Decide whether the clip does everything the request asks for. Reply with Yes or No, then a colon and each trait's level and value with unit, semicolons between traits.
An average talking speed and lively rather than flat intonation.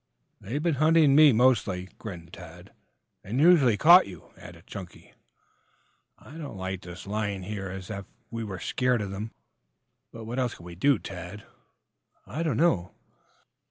Yes: average, 160 wpm; wide, 6.4 semitones